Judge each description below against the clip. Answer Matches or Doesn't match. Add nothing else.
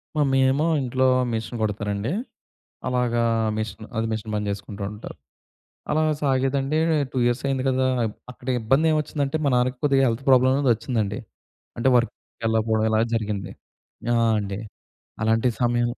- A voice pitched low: Matches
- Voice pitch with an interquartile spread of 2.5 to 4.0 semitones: Matches